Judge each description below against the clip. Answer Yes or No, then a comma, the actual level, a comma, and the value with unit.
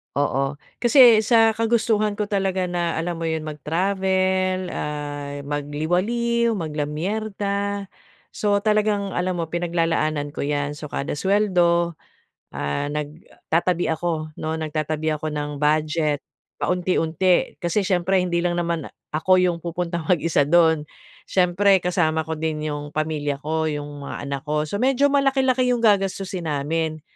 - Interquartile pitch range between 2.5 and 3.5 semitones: No, average, 4.2 semitones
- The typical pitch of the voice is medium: Yes, medium, 170 Hz